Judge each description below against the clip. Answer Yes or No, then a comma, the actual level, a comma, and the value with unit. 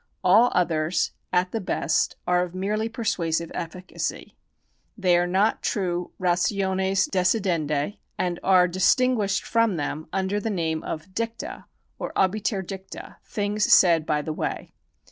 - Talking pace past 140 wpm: No, slow, 135 wpm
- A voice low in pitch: No, medium, 185 Hz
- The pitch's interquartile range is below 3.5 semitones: Yes, average, 2.8 semitones